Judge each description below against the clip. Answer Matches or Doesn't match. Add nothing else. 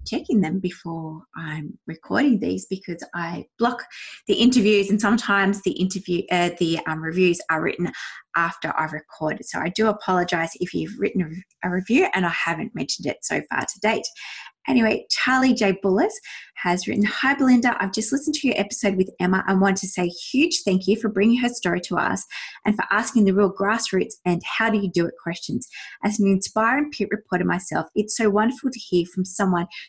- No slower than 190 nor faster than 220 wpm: Matches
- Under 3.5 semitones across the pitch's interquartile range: Doesn't match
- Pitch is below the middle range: Doesn't match